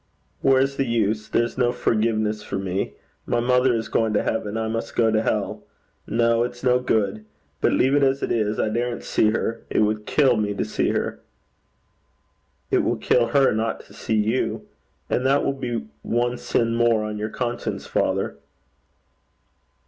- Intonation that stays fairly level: Yes, narrow, 2.3 semitones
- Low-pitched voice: Yes, low, 115 Hz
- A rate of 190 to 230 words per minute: No, average, 180 wpm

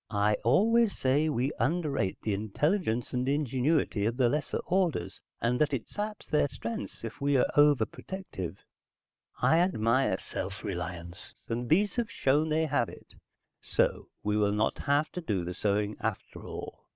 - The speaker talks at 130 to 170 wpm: Yes, average, 160 wpm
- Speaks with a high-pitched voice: No, low, 125 Hz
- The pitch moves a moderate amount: No, wide, 6.6 semitones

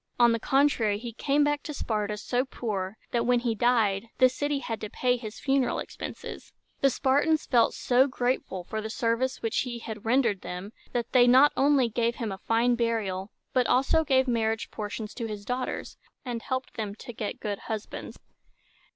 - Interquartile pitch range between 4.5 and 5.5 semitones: No, average, 3.1 semitones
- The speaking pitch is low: No, high, 235 Hz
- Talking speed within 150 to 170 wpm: No, average, 185 wpm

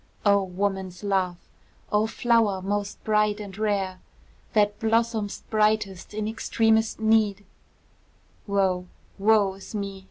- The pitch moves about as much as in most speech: No, narrow, 2.0 semitones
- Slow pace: Yes, slow, 115 wpm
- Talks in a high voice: Yes, high, 205 Hz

